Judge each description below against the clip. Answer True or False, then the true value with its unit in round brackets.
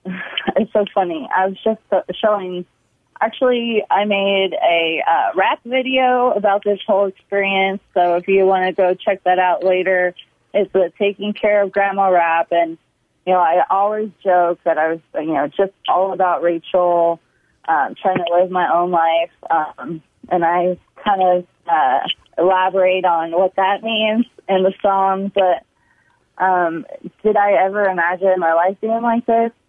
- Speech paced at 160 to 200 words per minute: True (165 wpm)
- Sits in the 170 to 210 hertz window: True (190 Hz)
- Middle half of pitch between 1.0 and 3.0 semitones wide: True (2.4 semitones)